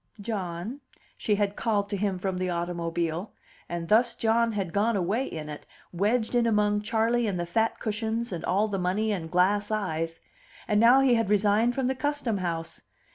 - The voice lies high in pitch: Yes, high, 205 Hz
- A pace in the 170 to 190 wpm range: Yes, average, 185 wpm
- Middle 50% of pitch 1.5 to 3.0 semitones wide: No, average, 4.0 semitones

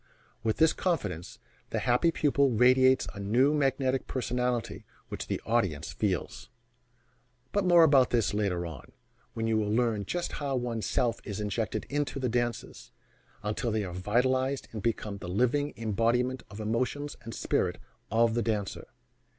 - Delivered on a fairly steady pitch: No, average, 3.7 semitones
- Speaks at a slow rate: No, average, 160 wpm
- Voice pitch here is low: Yes, low, 120 Hz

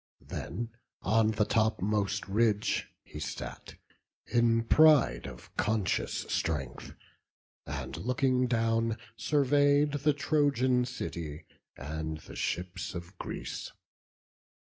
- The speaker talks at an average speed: No, slow, 100 wpm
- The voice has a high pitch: No, low, 115 Hz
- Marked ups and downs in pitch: Yes, wide, 5.8 semitones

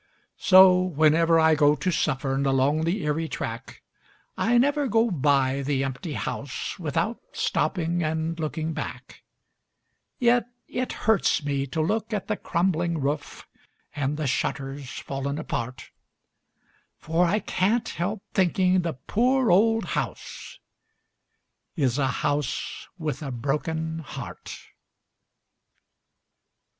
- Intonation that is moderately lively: Yes, average, 4.9 semitones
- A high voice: No, medium, 160 Hz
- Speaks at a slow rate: Yes, slow, 120 wpm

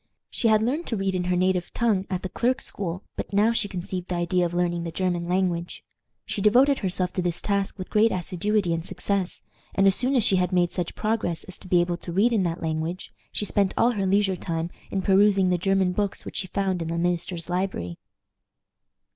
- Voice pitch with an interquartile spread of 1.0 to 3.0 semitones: Yes, narrow, 2.4 semitones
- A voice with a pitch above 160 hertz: Yes, medium, 185 Hz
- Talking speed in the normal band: No, fast, 220 wpm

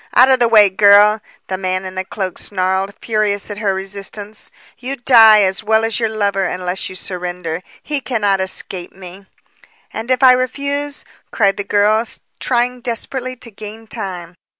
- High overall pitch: Yes, high, 205 Hz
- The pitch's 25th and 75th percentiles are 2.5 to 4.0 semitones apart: Yes, average, 3.5 semitones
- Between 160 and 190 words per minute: Yes, average, 170 wpm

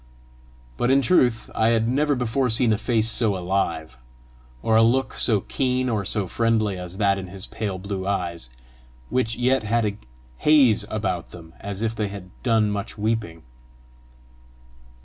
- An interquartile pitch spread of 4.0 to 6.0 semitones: No, average, 3.3 semitones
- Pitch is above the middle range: No, low, 110 Hz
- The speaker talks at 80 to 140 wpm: No, average, 165 wpm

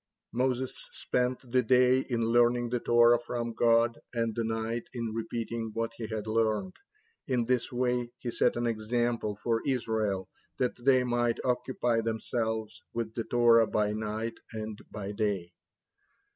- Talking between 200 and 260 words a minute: No, average, 150 wpm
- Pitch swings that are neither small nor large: No, narrow, 1.6 semitones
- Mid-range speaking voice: No, low, 115 Hz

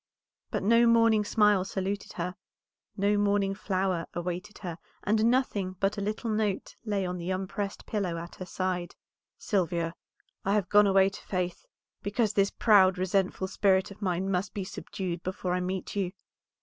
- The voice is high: Yes, high, 195 Hz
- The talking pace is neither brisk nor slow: Yes, average, 165 wpm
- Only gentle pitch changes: Yes, narrow, 2.1 semitones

